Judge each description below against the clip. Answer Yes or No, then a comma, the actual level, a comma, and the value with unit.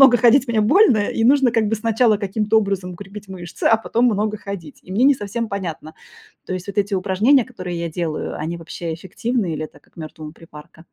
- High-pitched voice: Yes, high, 200 Hz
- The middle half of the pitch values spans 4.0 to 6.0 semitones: Yes, average, 4.5 semitones